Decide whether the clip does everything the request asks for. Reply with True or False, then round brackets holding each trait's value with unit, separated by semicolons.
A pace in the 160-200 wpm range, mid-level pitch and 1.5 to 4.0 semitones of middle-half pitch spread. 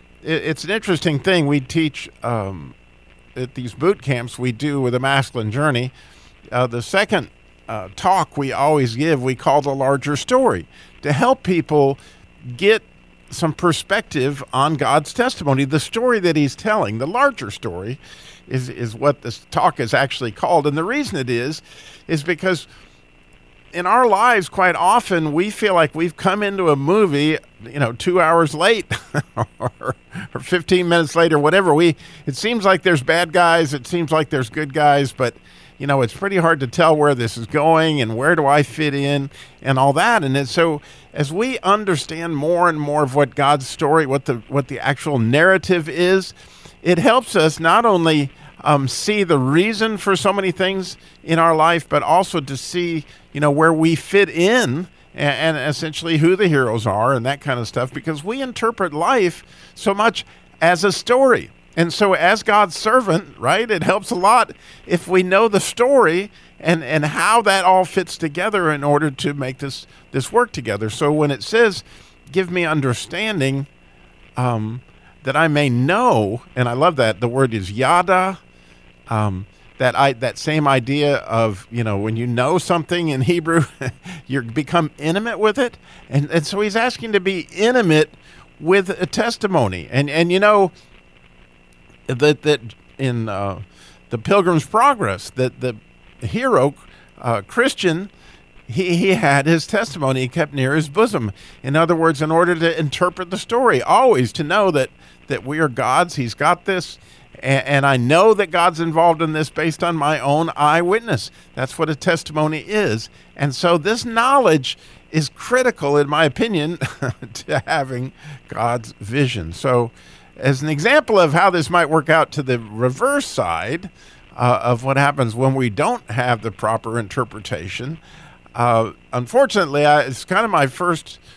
False (170 wpm; 150 Hz; 5.6 semitones)